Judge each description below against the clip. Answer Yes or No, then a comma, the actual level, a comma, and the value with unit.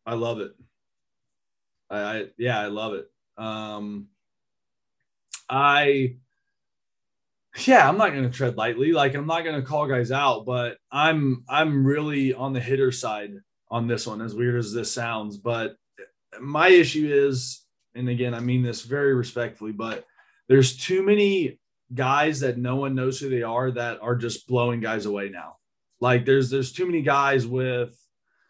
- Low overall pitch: Yes, low, 125 Hz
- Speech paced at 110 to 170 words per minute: Yes, average, 165 wpm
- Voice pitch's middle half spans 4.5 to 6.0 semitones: No, average, 2.9 semitones